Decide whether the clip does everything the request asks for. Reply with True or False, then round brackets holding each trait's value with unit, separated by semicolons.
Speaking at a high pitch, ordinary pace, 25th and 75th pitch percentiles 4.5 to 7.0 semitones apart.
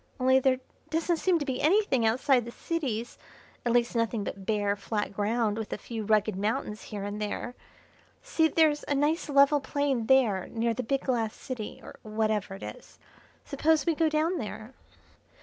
True (245 Hz; 180 wpm; 5.1 semitones)